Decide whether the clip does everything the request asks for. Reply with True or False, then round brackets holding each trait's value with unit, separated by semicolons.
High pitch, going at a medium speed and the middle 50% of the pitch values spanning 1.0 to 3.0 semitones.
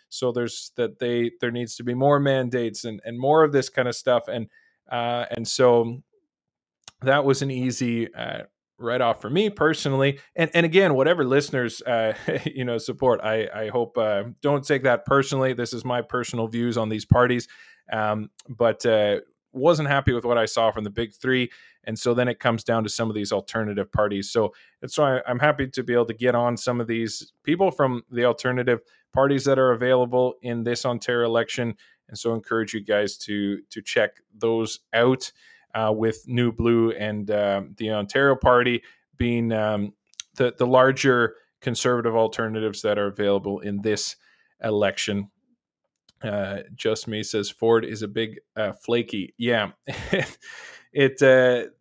False (120 Hz; 180 wpm; 2.6 semitones)